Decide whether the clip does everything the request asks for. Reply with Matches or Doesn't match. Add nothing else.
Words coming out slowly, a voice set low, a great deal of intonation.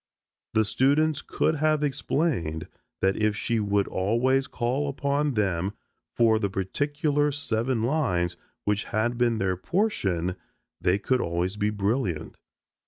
Matches